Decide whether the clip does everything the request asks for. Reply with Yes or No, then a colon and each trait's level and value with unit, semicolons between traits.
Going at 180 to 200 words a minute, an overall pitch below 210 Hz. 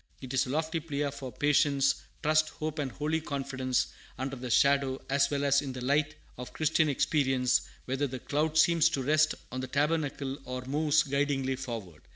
Yes: average, 185 wpm; medium, 140 Hz